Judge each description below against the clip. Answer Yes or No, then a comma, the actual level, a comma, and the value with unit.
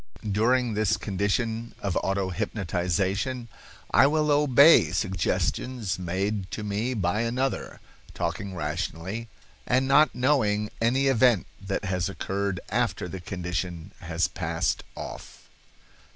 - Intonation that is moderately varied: Yes, average, 4.8 semitones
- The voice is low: Yes, low, 105 Hz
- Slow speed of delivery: Yes, slow, 115 wpm